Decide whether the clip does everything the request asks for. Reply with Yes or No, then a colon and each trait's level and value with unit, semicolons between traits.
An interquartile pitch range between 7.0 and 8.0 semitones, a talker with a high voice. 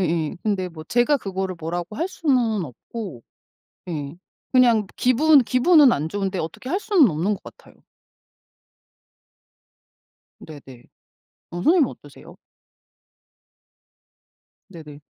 Yes: wide, 7.7 semitones; high, 195 Hz